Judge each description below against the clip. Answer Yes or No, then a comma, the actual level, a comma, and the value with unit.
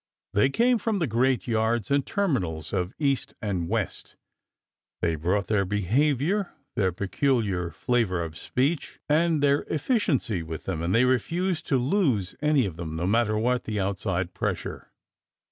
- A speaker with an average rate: Yes, average, 155 wpm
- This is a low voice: Yes, low, 115 Hz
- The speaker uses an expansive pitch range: Yes, wide, 7.3 semitones